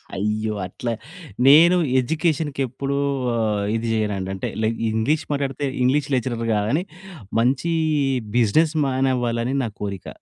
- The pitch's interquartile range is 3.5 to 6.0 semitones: Yes, average, 4.4 semitones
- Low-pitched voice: Yes, low, 125 Hz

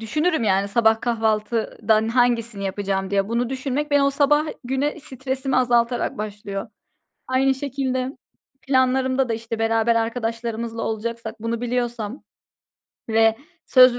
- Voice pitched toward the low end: No, high, 235 Hz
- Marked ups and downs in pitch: No, average, 2.7 semitones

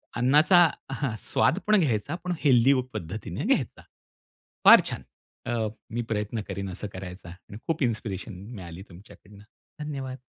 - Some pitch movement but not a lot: No, wide, 6.1 semitones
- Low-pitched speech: Yes, low, 110 Hz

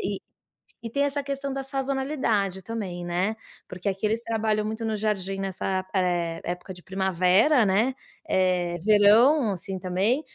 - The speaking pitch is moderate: No, high, 205 Hz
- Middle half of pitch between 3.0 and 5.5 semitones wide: Yes, average, 4.0 semitones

